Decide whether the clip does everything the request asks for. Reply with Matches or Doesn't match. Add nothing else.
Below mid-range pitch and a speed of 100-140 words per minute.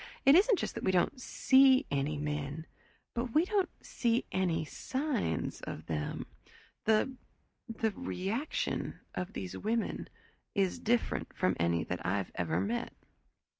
Doesn't match